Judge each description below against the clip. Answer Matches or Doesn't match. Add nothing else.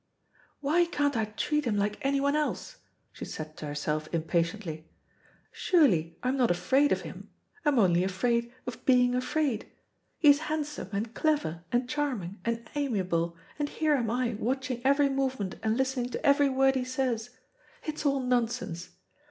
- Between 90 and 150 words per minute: Doesn't match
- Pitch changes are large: Matches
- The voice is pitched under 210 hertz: Doesn't match